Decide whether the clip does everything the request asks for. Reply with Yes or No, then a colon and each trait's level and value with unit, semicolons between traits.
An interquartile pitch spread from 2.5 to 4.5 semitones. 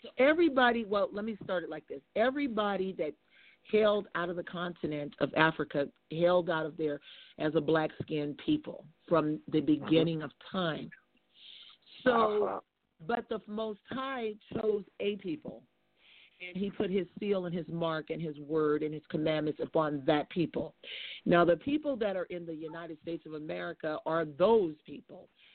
No: average, 5.1 semitones